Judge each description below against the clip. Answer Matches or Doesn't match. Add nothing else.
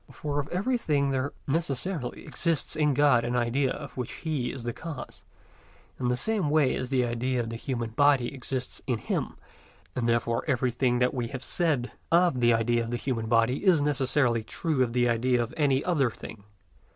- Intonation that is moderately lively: Matches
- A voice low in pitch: Matches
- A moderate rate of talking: Matches